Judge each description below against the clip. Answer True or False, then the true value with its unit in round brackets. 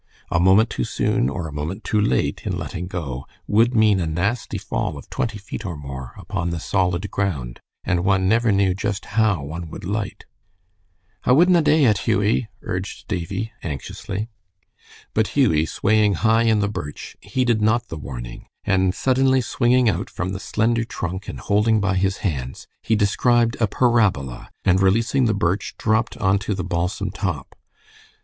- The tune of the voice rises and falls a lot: False (4.3 semitones)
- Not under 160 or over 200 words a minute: True (170 wpm)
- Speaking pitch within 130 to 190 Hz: False (100 Hz)